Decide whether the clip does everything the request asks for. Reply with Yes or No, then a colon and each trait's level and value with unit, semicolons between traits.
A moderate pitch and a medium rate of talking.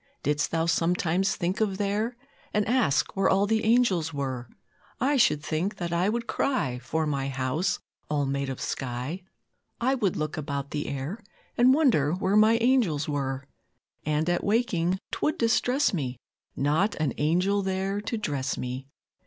Yes: medium, 175 Hz; average, 160 wpm